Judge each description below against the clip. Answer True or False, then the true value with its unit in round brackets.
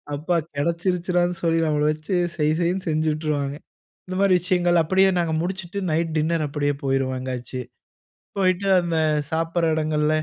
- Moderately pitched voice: True (165 Hz)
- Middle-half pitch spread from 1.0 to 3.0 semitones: True (2.7 semitones)